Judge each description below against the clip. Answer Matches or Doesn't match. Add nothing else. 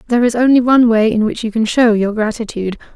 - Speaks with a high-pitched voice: Matches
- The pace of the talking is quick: Matches